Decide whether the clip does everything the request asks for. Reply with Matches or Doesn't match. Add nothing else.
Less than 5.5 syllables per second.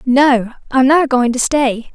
Matches